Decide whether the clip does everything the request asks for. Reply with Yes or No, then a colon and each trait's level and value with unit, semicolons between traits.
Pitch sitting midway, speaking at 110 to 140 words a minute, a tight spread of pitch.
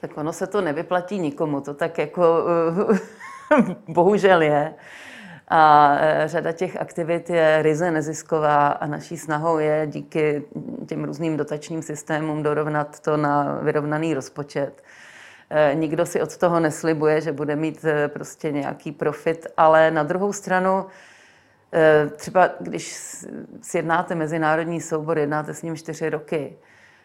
Yes: medium, 160 Hz; average, 125 wpm; narrow, 2.0 semitones